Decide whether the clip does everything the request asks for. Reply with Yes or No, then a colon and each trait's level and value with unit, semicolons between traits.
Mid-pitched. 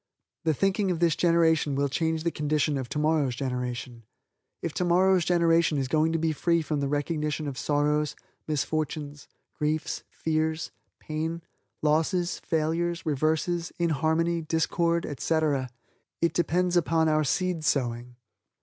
Yes: medium, 155 Hz